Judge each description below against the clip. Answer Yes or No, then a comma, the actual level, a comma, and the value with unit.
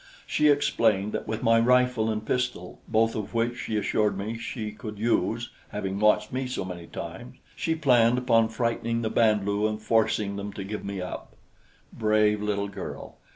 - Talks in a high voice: No, low, 110 Hz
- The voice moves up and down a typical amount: No, narrow, 2.1 semitones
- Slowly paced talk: No, average, 180 wpm